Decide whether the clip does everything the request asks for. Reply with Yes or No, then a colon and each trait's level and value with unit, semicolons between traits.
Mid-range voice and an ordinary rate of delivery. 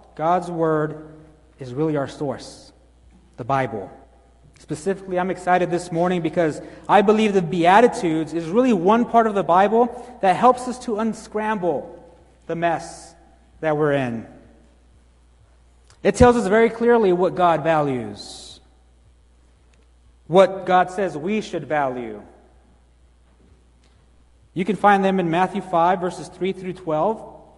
No: medium, 170 Hz; slow, 130 wpm